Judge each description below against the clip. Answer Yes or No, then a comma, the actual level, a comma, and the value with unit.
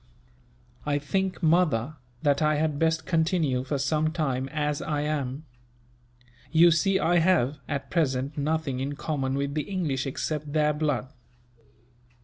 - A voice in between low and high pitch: Yes, medium, 150 Hz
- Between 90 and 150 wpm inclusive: Yes, average, 140 wpm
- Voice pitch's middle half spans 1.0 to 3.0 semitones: Yes, narrow, 2.5 semitones